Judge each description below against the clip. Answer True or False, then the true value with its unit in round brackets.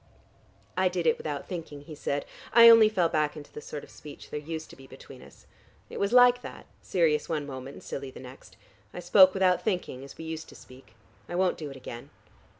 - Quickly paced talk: True (230 wpm)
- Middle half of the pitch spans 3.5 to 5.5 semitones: True (4.4 semitones)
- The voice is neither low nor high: True (160 Hz)